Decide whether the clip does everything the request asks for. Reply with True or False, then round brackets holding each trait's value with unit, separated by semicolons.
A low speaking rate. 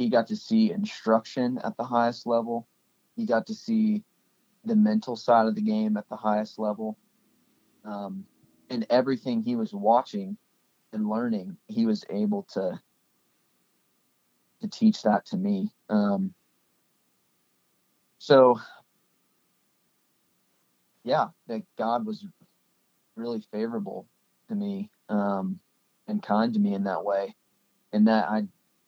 True (125 wpm)